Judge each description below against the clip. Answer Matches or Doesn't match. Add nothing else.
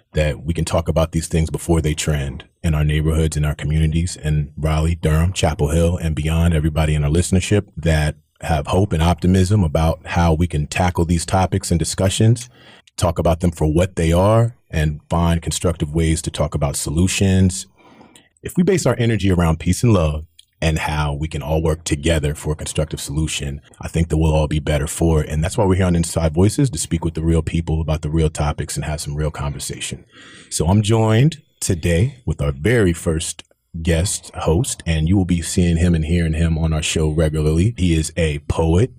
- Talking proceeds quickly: Matches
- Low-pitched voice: Matches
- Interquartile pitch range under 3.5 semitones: Matches